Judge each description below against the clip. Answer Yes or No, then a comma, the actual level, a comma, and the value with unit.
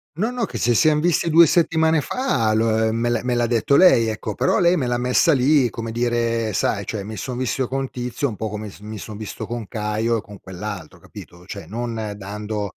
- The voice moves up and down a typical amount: Yes, average, 3.7 semitones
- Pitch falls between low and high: No, low, 115 Hz